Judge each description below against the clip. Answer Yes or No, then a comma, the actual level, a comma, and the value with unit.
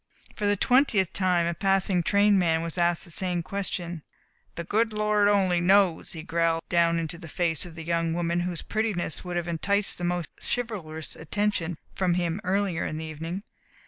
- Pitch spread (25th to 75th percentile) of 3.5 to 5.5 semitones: No, average, 3.1 semitones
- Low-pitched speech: No, medium, 175 Hz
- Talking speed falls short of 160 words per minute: No, average, 185 wpm